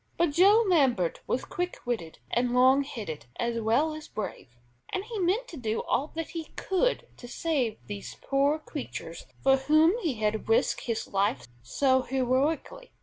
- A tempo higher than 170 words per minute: No, average, 165 wpm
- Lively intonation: Yes, wide, 6.5 semitones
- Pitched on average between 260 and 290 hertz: Yes, very high, 265 Hz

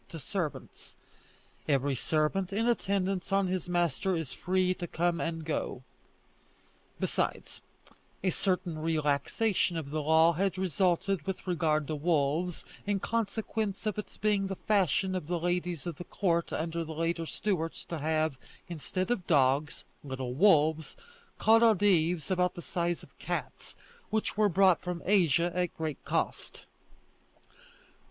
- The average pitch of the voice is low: No, medium, 175 Hz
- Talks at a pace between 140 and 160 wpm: Yes, average, 145 wpm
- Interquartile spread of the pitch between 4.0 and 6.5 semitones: No, average, 3.4 semitones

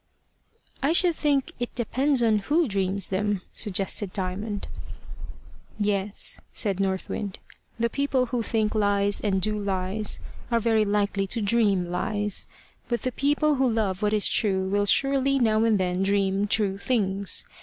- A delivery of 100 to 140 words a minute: No, average, 160 wpm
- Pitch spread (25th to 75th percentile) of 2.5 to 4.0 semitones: Yes, average, 3.1 semitones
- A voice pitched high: Yes, high, 210 Hz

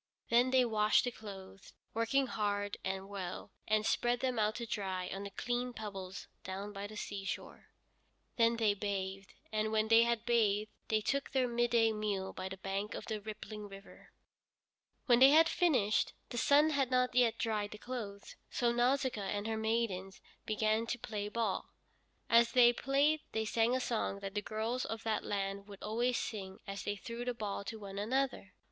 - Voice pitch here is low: No, high, 220 Hz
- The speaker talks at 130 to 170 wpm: No, average, 185 wpm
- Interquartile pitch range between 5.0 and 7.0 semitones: No, average, 3.0 semitones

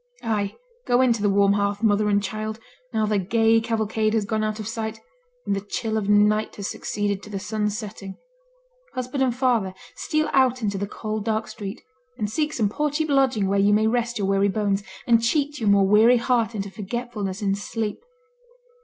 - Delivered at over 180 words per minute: Yes, average, 200 wpm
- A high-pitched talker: Yes, high, 215 Hz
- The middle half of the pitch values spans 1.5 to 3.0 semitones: Yes, narrow, 2.5 semitones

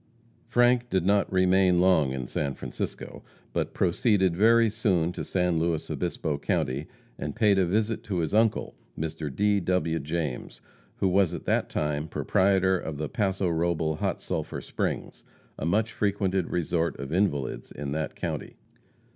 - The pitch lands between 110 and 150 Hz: No, very low, 90 Hz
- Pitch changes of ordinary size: Yes, average, 3.9 semitones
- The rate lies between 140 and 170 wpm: Yes, average, 155 wpm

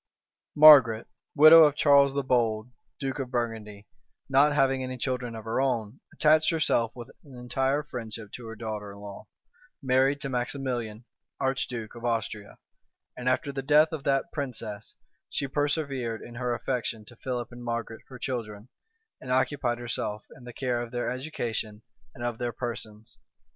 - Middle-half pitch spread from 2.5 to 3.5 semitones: Yes, average, 3.1 semitones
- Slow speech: No, average, 165 wpm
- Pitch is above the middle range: No, low, 125 Hz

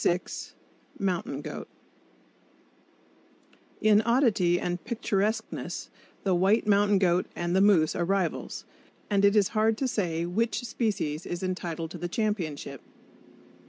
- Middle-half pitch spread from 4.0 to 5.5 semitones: No, average, 3.6 semitones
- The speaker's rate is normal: No, slow, 125 wpm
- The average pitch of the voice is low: No, high, 195 Hz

